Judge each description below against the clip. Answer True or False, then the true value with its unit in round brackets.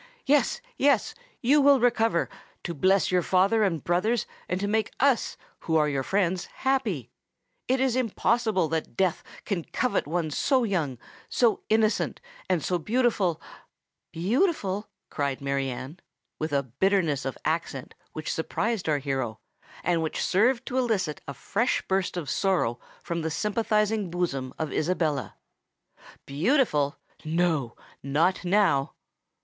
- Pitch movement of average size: False (6.5 semitones)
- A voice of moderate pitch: True (180 Hz)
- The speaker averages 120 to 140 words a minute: True (135 wpm)